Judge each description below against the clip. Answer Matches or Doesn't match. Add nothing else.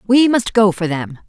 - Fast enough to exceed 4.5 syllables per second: Matches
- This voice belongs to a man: Doesn't match